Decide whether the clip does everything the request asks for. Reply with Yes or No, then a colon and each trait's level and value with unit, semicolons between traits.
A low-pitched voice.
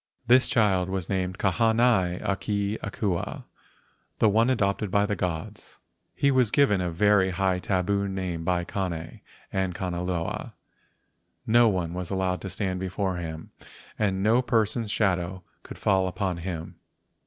Yes: very low, 95 Hz